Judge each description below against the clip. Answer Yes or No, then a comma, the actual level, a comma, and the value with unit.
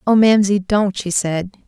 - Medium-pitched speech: No, high, 195 Hz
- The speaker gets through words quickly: No, average, 180 wpm